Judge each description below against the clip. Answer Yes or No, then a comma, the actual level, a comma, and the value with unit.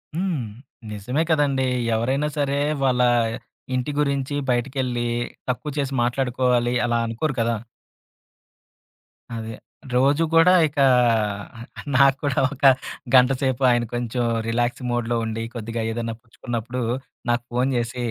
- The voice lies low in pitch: Yes, low, 125 Hz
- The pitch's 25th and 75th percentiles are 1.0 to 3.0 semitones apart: Yes, narrow, 2.5 semitones